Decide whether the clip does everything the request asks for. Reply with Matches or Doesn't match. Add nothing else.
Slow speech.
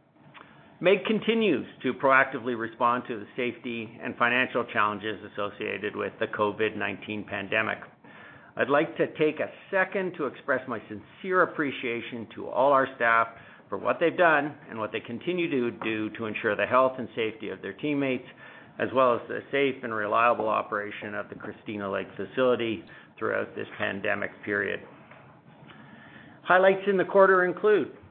Doesn't match